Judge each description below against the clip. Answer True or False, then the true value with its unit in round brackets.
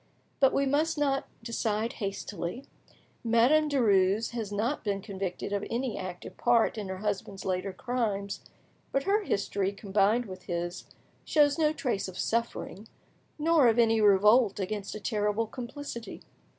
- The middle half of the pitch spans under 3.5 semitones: False (4.2 semitones)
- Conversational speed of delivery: True (145 wpm)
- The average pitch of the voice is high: True (220 Hz)